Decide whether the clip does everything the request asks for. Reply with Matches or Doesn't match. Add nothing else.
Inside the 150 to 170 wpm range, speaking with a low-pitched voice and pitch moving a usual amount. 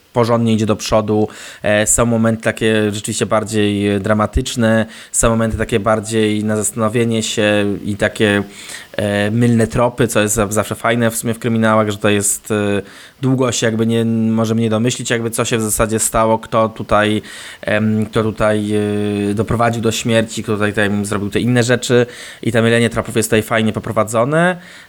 Doesn't match